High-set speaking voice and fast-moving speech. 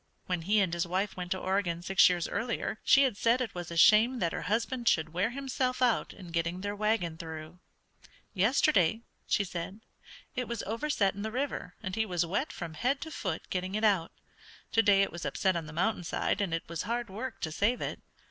Yes: high, 195 Hz; fast, 215 wpm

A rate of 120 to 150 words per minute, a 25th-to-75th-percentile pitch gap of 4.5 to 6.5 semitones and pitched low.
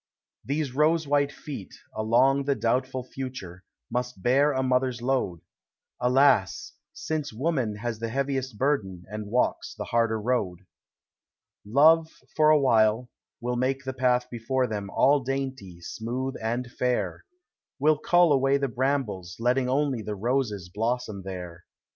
No: average, 140 wpm; average, 3.9 semitones; low, 125 Hz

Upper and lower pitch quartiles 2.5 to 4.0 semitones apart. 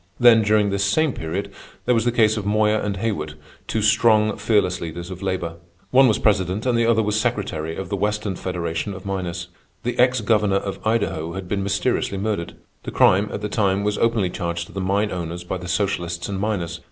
Yes: average, 3.2 semitones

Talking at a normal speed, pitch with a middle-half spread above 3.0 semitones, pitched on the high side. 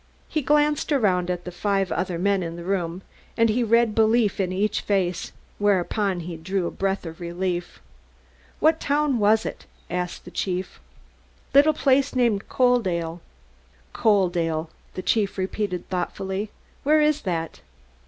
Yes: average, 145 wpm; average, 4.6 semitones; high, 195 Hz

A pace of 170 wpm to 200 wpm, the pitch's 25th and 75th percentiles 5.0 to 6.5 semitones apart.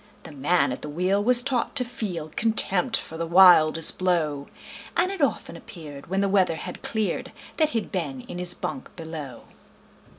Yes: average, 175 wpm; wide, 5.4 semitones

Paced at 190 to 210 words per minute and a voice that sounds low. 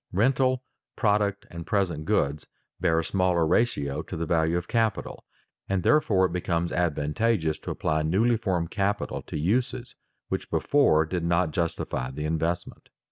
No: average, 150 wpm; very low, 90 Hz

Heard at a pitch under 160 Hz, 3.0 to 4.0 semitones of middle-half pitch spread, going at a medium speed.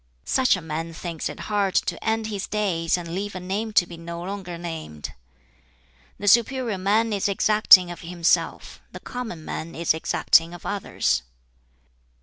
No: medium, 185 Hz; average, 3.7 semitones; average, 160 wpm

